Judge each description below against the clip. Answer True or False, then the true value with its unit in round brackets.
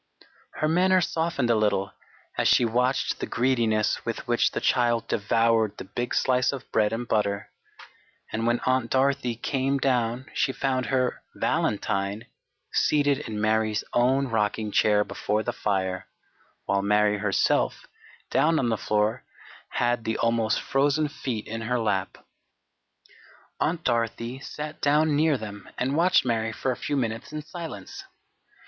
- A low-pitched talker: True (120 Hz)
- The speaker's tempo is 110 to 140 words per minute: False (150 wpm)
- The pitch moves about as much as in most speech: True (4.0 semitones)